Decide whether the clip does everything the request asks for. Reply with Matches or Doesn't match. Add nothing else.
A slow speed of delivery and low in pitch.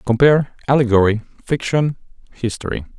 Matches